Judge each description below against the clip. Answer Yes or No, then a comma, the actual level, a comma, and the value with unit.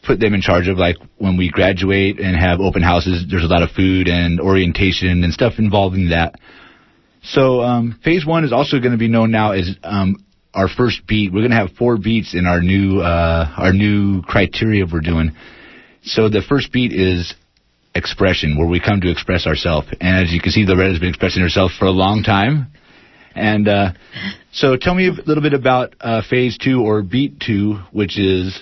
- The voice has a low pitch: Yes, very low, 95 Hz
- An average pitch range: Yes, average, 3.7 semitones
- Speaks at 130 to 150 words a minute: No, fast, 205 wpm